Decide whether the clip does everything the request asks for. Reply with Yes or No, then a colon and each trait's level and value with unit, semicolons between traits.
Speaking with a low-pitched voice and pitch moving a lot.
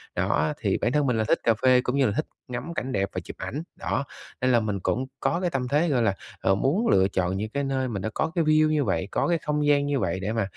Yes: low, 130 Hz; wide, 6.0 semitones